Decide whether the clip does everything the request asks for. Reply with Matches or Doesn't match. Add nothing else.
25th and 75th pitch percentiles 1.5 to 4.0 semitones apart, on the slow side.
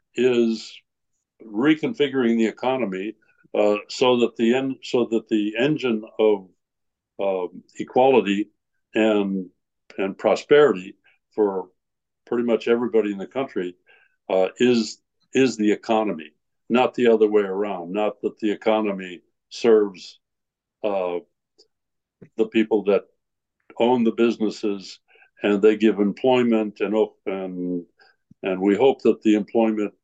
Matches